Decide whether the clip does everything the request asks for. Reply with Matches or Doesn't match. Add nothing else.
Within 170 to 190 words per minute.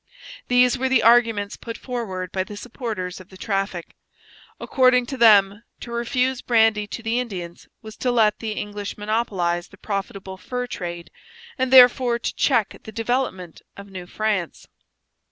Doesn't match